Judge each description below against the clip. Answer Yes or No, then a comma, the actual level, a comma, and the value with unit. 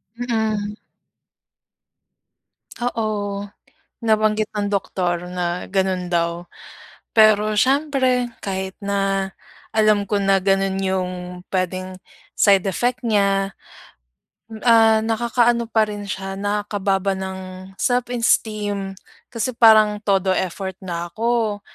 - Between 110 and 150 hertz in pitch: No, high, 205 Hz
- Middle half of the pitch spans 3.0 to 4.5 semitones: No, narrow, 2.4 semitones